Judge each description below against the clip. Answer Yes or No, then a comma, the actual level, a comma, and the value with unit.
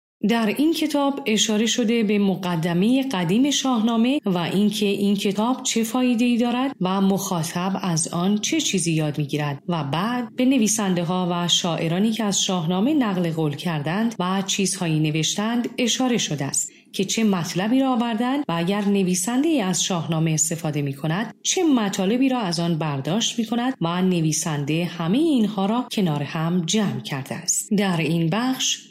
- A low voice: No, high, 200 Hz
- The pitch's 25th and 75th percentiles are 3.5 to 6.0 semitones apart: Yes, wide, 5.5 semitones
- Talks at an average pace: No, fast, 160 wpm